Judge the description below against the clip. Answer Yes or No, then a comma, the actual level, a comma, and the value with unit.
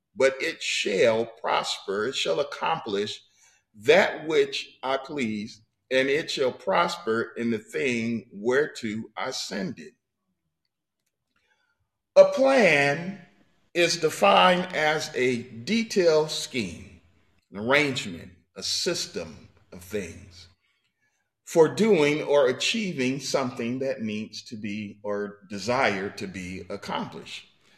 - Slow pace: Yes, slow, 110 wpm